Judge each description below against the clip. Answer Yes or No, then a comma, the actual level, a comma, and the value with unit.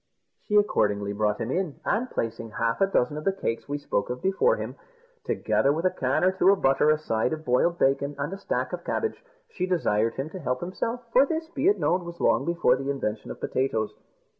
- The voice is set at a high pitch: No, medium, 150 Hz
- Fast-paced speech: Yes, fast, 225 wpm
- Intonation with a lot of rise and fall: Yes, wide, 7.4 semitones